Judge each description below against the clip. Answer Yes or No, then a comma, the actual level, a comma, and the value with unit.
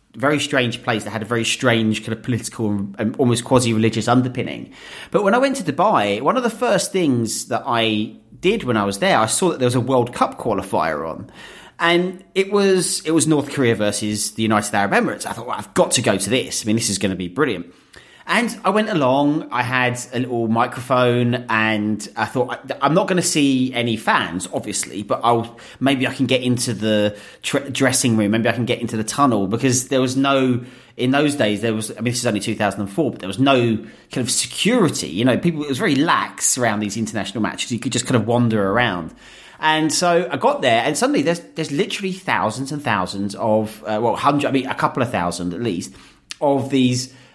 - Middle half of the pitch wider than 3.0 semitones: Yes, average, 3.9 semitones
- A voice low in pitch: Yes, low, 120 Hz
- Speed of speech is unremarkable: No, fast, 225 wpm